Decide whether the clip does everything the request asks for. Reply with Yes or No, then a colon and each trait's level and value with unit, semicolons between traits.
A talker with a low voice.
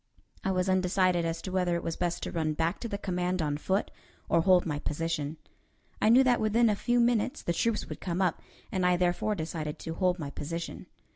No: medium, 180 Hz